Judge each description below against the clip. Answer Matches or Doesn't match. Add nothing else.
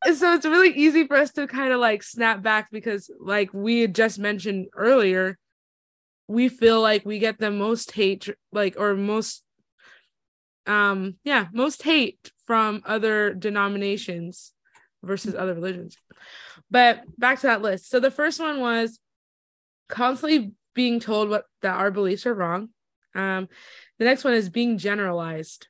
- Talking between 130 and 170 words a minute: Matches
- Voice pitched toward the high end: Matches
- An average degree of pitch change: Matches